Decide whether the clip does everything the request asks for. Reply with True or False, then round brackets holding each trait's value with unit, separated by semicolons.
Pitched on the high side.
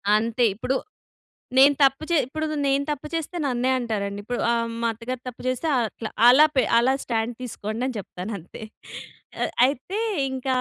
True (245 Hz)